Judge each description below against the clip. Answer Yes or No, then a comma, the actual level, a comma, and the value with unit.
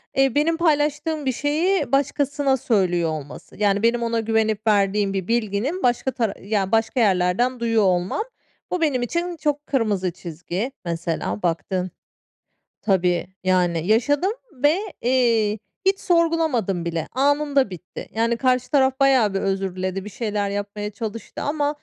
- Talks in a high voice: Yes, high, 225 Hz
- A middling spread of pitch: No, wide, 6.3 semitones